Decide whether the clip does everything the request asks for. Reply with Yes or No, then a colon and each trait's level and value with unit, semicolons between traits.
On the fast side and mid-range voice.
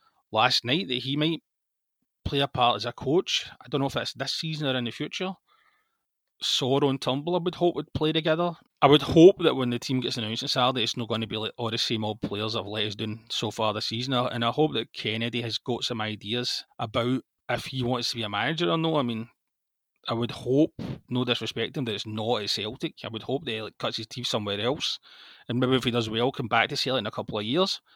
No: fast, 255 wpm; low, 125 Hz